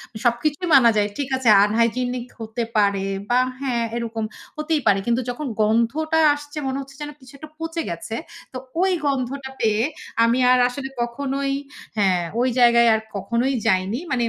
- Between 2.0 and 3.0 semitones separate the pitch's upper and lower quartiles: No, average, 3.5 semitones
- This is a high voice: Yes, high, 245 Hz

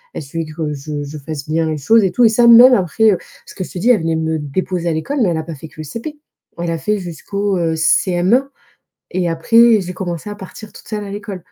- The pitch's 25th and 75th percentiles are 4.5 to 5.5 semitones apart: Yes, average, 4.9 semitones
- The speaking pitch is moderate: Yes, medium, 175 Hz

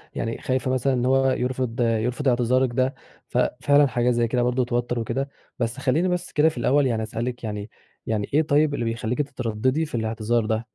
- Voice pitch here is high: No, low, 125 Hz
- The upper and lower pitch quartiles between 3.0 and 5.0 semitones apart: No, narrow, 2.5 semitones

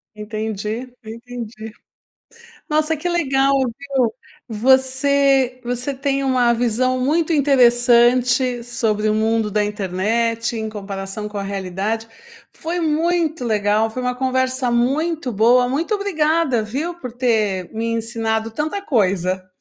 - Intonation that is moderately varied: Yes, average, 3.9 semitones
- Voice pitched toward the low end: No, high, 240 Hz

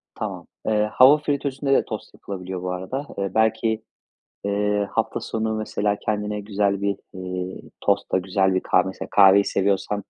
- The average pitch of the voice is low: Yes, low, 100 Hz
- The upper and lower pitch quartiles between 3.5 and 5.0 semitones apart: No, narrow, 2.5 semitones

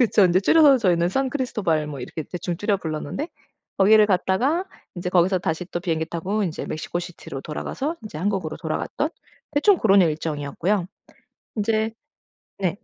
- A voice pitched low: No, high, 190 Hz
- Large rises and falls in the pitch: No, average, 4.5 semitones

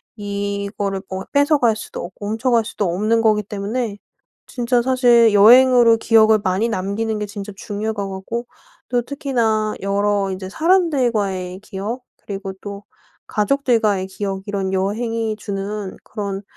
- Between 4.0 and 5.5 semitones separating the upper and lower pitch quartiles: No, average, 2.9 semitones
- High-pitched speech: Yes, high, 210 Hz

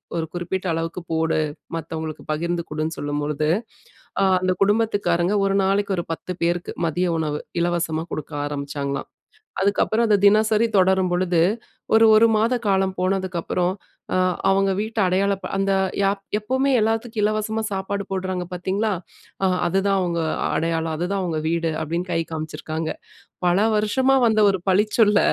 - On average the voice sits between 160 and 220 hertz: Yes, medium, 185 Hz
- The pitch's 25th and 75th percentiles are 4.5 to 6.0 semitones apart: No, average, 3.7 semitones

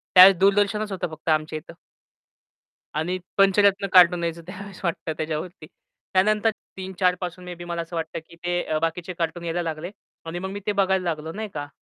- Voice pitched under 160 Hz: No, medium, 175 Hz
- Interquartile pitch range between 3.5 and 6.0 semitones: No, narrow, 2.6 semitones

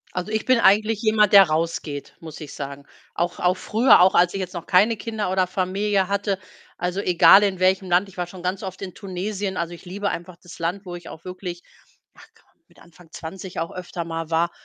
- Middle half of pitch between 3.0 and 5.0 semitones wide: No, narrow, 2.4 semitones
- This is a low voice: No, medium, 185 Hz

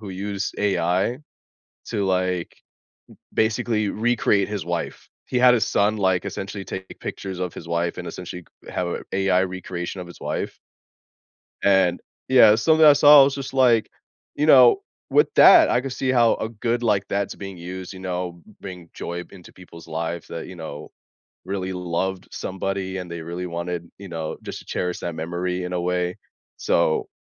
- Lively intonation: No, average, 3.3 semitones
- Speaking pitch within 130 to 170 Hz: No, very low, 95 Hz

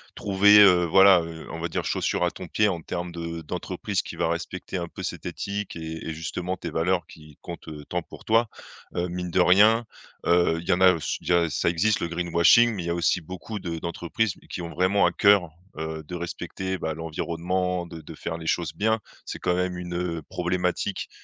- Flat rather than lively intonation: Yes, narrow, 1.9 semitones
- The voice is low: Yes, very low, 90 Hz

